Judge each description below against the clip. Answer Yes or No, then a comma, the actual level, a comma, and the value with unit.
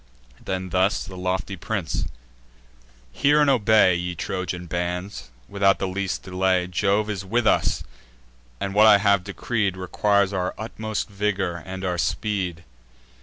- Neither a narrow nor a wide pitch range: No, narrow, 2.3 semitones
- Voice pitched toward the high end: No, very low, 95 Hz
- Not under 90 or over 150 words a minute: Yes, average, 140 wpm